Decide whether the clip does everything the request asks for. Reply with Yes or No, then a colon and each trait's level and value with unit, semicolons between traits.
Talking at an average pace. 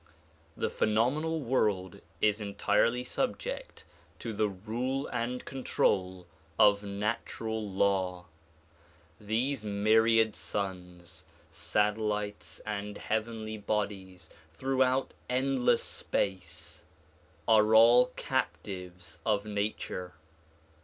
No: slow, 85 wpm